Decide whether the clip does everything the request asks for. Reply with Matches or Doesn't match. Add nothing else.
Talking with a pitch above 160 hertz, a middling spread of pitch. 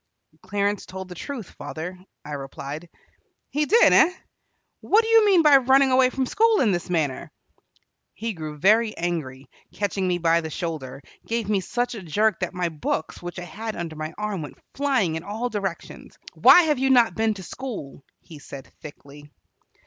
Doesn't match